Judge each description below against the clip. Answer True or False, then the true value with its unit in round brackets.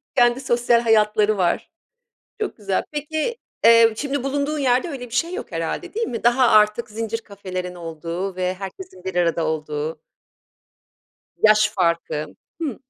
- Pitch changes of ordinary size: False (6.1 semitones)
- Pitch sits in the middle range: False (215 Hz)